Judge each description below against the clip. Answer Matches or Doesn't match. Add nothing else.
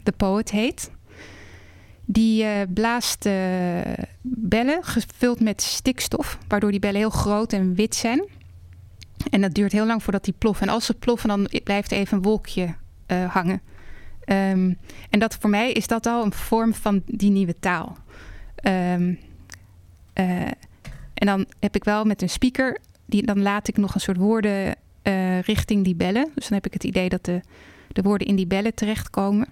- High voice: Matches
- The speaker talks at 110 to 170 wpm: Doesn't match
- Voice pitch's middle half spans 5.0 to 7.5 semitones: Doesn't match